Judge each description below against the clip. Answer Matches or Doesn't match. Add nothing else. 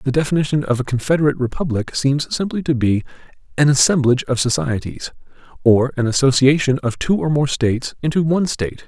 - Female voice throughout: Doesn't match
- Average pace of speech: Matches